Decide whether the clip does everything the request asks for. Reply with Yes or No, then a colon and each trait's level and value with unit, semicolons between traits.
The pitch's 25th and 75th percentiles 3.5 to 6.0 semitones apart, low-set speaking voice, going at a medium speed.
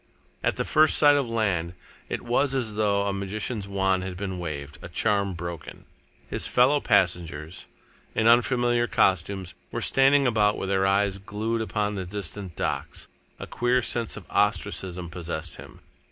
Yes: average, 4.1 semitones; low, 100 Hz; average, 160 wpm